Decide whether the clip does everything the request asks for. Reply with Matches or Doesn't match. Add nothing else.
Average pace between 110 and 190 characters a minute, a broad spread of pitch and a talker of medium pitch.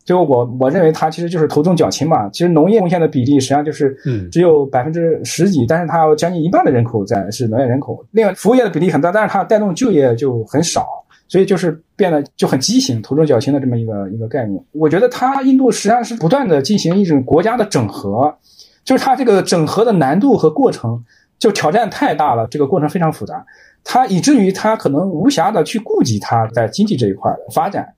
Doesn't match